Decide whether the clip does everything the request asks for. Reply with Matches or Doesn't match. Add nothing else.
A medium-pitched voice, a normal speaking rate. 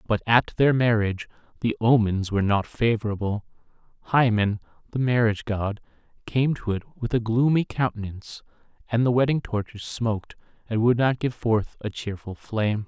Doesn't match